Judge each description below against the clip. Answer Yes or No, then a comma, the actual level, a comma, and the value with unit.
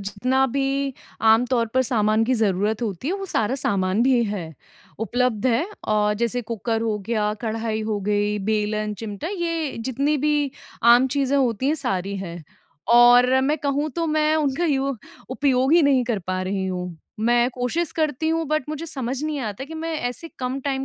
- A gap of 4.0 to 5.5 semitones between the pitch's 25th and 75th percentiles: Yes, average, 4.7 semitones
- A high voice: Yes, high, 245 Hz